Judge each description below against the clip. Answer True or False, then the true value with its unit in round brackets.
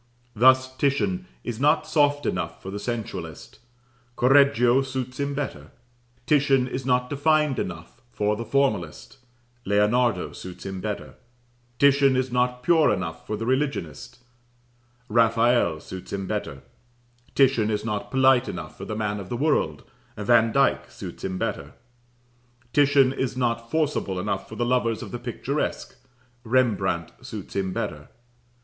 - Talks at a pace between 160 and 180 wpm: False (140 wpm)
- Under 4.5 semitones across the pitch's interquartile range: False (4.8 semitones)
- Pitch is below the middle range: True (120 Hz)